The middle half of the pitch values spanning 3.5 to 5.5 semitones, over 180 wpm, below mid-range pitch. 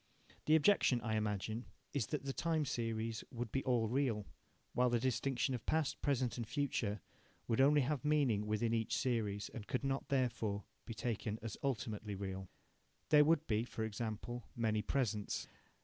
No: average, 3.9 semitones; average, 165 wpm; low, 120 Hz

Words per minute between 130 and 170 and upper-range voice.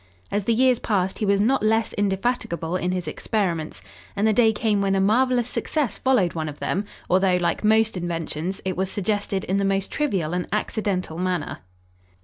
No: average, 185 wpm; high, 195 Hz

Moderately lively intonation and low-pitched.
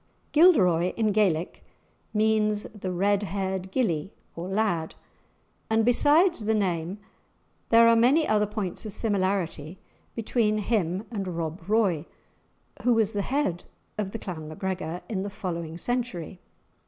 No: average, 3.7 semitones; high, 200 Hz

